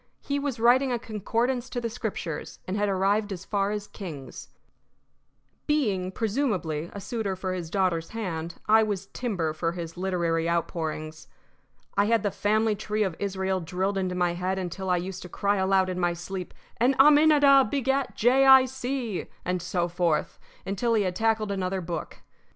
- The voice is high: Yes, high, 195 Hz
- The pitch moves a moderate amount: Yes, average, 4.1 semitones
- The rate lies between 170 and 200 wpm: Yes, average, 175 wpm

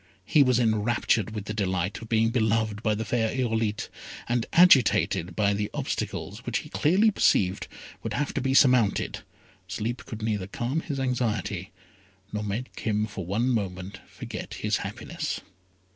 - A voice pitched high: No, low, 110 Hz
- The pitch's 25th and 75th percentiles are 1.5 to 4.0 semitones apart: Yes, average, 3.2 semitones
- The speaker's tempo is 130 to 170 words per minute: Yes, average, 160 wpm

